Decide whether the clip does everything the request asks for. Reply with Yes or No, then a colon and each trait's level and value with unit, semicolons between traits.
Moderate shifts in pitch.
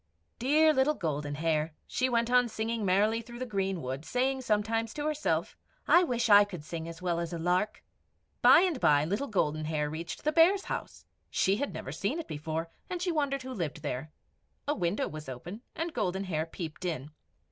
No: wide, 8.1 semitones